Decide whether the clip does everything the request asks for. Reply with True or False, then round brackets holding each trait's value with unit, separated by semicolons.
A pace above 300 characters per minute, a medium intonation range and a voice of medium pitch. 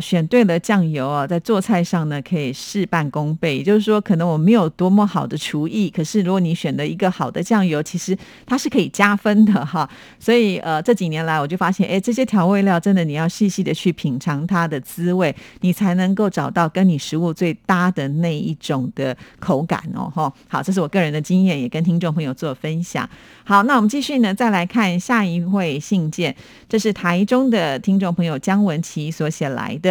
True (315 characters per minute; 4.0 semitones; 180 Hz)